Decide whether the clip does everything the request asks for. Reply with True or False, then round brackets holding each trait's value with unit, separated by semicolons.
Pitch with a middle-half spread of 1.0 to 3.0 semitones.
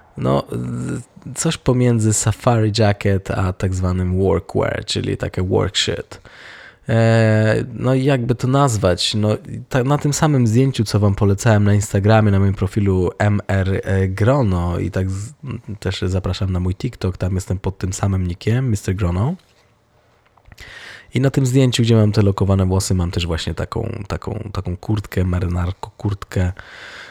False (3.9 semitones)